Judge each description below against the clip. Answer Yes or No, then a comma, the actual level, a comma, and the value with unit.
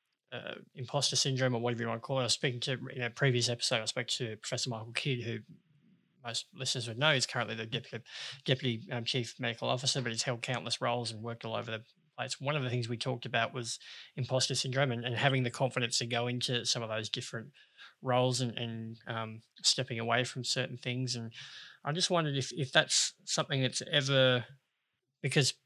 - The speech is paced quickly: Yes, fast, 215 wpm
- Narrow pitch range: Yes, narrow, 2.2 semitones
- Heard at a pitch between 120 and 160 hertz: Yes, low, 125 Hz